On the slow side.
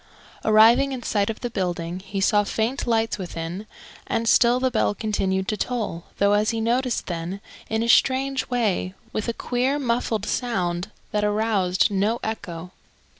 No: average, 165 wpm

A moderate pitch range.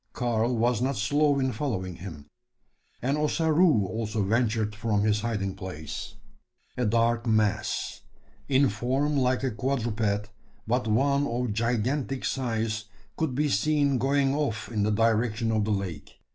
Yes: average, 4.0 semitones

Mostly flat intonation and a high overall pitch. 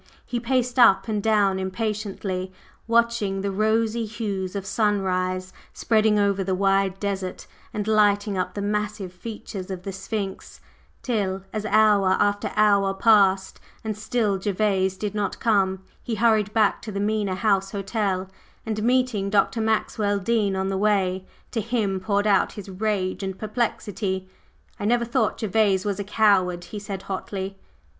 Yes: narrow, 2.1 semitones; high, 205 Hz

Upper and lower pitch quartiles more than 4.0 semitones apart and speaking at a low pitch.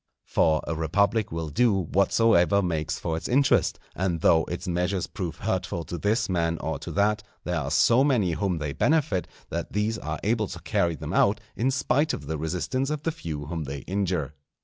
Yes: average, 5.2 semitones; very low, 90 Hz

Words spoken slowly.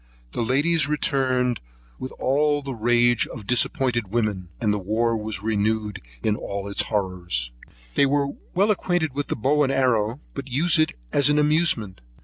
No: average, 165 wpm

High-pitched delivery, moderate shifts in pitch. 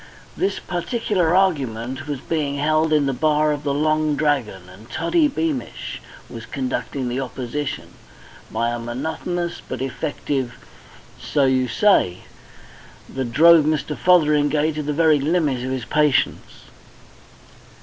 No: medium, 150 Hz; average, 3.4 semitones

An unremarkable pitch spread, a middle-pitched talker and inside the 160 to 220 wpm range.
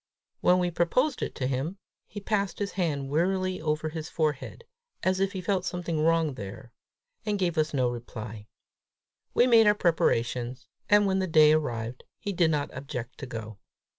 No: wide, 6.4 semitones; medium, 160 Hz; average, 175 wpm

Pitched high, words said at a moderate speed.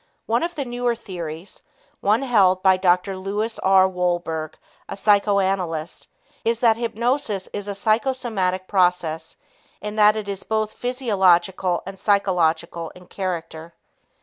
No: high, 195 Hz; slow, 130 wpm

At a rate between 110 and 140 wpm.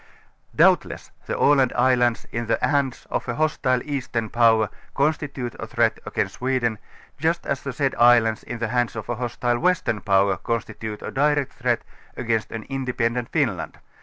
No: average, 165 wpm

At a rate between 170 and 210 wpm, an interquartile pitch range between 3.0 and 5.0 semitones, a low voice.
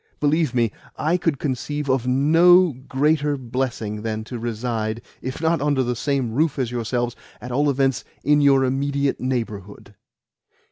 No: average, 150 wpm; average, 3.4 semitones; low, 130 Hz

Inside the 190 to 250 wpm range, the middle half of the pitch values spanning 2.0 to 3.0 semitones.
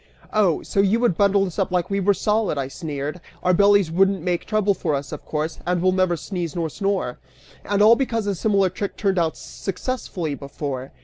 No: fast, 205 wpm; average, 3.7 semitones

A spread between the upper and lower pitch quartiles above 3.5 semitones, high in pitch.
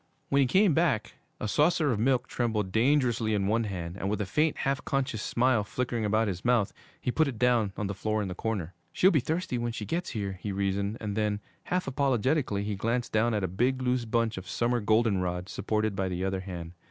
No: average, 4.1 semitones; low, 110 Hz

